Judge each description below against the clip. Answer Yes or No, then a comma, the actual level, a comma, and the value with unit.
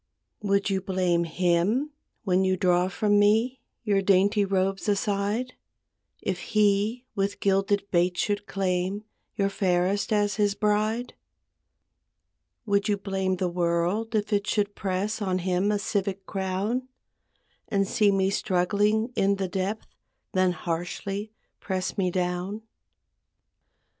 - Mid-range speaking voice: No, high, 195 Hz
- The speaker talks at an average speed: No, slow, 130 wpm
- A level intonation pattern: Yes, narrow, 2.0 semitones